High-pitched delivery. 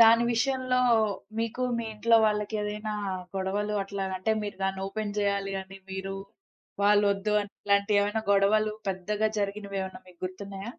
Yes: high, 205 Hz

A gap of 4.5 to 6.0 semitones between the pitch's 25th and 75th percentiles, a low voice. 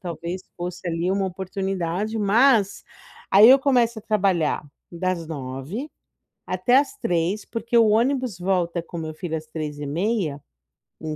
No: average, 4.8 semitones; medium, 185 Hz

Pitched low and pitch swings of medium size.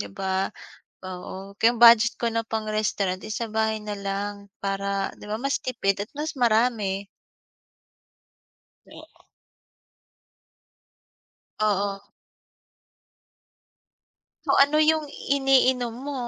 No: high, 215 Hz; average, 3.6 semitones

